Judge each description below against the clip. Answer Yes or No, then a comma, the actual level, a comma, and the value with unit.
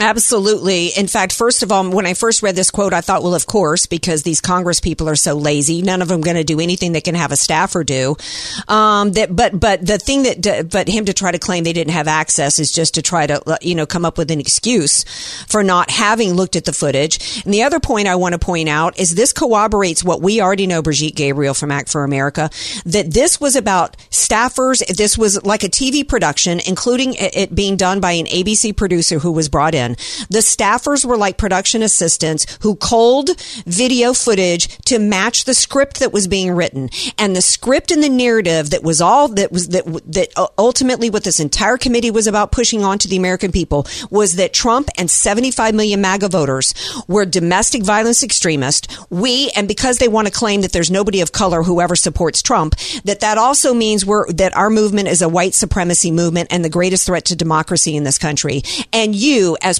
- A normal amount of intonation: Yes, average, 4.4 semitones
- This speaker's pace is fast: Yes, fast, 215 wpm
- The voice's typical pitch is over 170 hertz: Yes, high, 190 Hz